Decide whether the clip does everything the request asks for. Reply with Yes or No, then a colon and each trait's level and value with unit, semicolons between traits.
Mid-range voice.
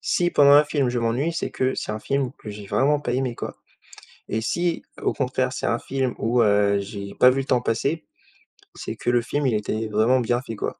No: low, 125 Hz